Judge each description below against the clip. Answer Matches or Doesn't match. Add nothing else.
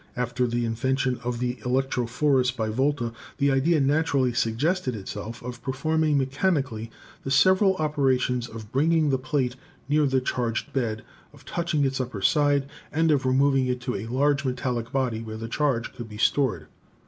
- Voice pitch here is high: Doesn't match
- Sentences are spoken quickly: Doesn't match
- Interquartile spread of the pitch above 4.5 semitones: Doesn't match